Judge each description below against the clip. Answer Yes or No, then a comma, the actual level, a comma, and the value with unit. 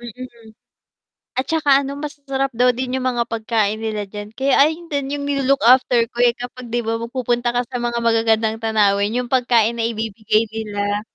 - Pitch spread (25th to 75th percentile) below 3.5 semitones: Yes, average, 2.7 semitones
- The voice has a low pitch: No, high, 240 Hz